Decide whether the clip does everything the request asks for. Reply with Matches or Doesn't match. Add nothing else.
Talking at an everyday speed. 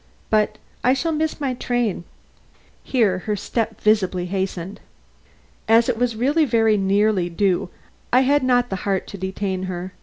Matches